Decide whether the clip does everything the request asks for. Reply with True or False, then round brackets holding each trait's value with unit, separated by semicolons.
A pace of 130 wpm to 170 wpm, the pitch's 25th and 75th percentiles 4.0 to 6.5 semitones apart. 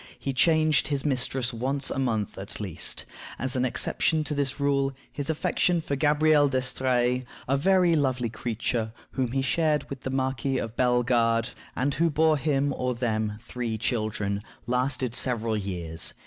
False (160 wpm; 3.5 semitones)